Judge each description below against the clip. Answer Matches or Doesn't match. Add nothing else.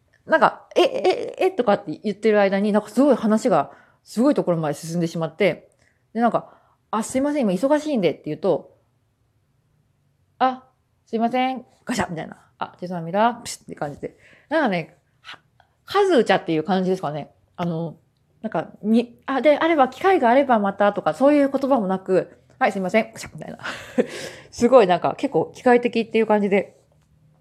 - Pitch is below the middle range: Doesn't match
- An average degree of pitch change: Doesn't match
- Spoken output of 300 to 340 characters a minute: Doesn't match